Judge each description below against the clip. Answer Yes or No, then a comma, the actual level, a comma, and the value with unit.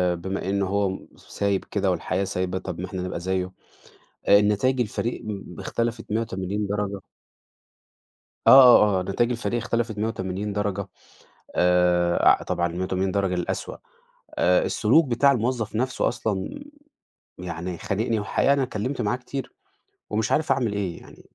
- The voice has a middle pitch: No, low, 100 Hz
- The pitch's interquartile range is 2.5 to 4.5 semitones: Yes, average, 3.9 semitones